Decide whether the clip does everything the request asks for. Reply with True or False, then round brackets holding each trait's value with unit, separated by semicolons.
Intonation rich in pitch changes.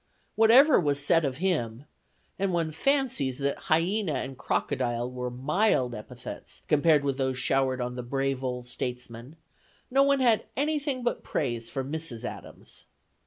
True (7.1 semitones)